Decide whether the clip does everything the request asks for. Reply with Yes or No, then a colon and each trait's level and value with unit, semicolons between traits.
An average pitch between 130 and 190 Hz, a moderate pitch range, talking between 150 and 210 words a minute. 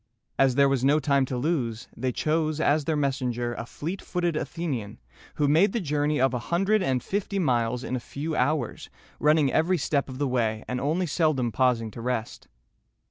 Yes: medium, 140 Hz; average, 4.0 semitones; average, 190 wpm